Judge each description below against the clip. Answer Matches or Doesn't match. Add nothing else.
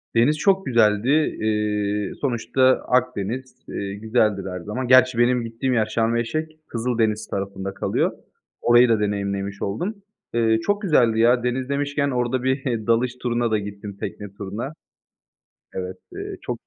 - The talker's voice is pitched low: Matches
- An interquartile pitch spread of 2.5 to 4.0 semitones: Matches